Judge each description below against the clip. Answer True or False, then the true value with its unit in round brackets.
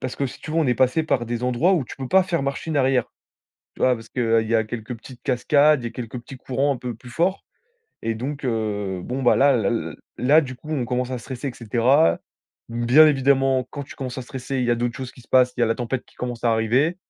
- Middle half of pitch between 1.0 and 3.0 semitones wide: True (2.7 semitones)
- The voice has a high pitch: False (125 Hz)